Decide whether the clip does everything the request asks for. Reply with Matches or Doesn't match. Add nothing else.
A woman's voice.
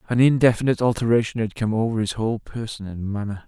Doesn't match